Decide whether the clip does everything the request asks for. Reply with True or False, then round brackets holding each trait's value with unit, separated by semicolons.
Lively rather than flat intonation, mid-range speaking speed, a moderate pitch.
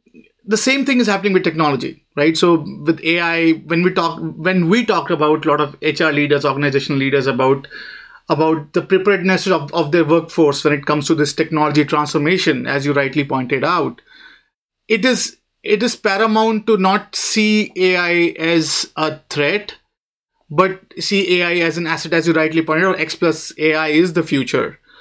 False (3.6 semitones; 180 wpm; 165 Hz)